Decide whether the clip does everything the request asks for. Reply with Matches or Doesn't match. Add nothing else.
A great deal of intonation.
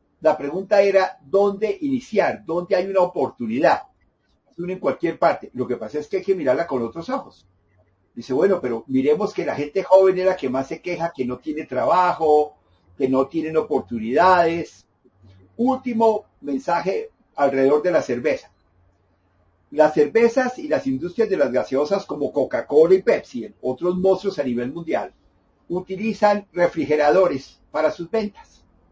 Matches